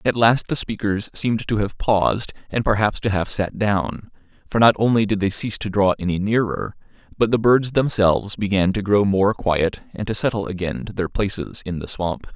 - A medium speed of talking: No, fast, 210 wpm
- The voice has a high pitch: No, low, 100 Hz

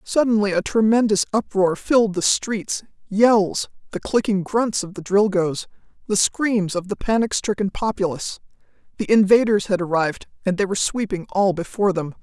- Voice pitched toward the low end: No, high, 200 Hz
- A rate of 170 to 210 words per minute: No, average, 155 wpm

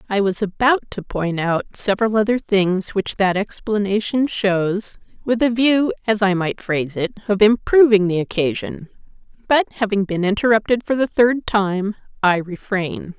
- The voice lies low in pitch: No, high, 205 Hz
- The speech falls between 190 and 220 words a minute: No, average, 160 wpm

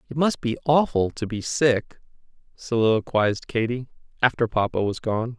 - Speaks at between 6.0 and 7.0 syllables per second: No, 4.9 syllables/s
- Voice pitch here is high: No, low, 120 Hz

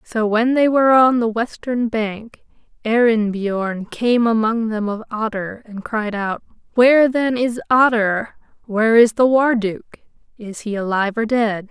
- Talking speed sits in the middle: Yes, average, 160 wpm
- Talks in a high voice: Yes, high, 225 Hz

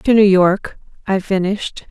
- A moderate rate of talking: Yes, average, 160 wpm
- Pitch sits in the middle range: No, high, 195 Hz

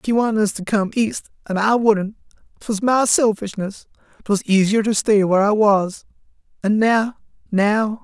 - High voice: Yes, high, 200 Hz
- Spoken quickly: No, average, 150 wpm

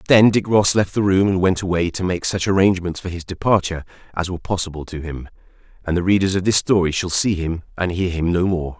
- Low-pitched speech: Yes, very low, 90 Hz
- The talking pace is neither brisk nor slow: No, fast, 240 wpm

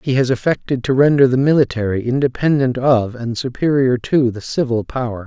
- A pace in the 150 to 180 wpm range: Yes, average, 170 wpm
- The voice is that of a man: Yes, male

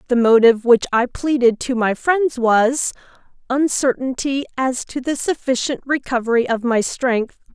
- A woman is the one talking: Yes, female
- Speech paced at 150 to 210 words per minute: No, slow, 135 wpm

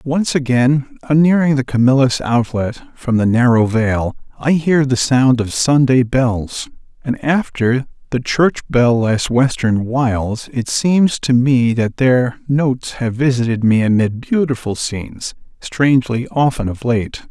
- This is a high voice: No, low, 130 Hz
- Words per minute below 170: Yes, average, 150 wpm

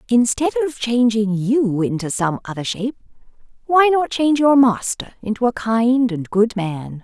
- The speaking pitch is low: No, high, 230 Hz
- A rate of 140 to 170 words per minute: Yes, average, 160 wpm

